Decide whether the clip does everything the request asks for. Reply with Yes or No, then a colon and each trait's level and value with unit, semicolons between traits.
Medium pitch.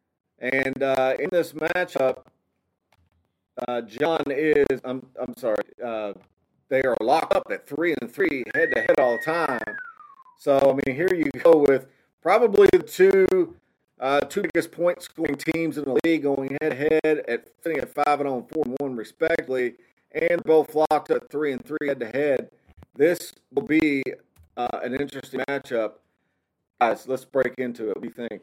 Yes: medium, 145 Hz